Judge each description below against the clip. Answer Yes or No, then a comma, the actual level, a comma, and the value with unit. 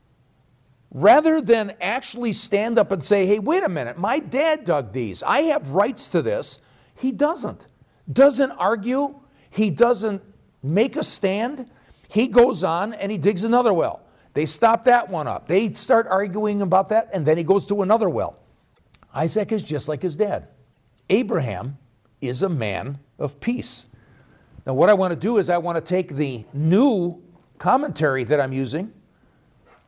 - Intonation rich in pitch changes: Yes, wide, 7.2 semitones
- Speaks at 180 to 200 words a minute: No, average, 165 wpm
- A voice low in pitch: No, high, 195 Hz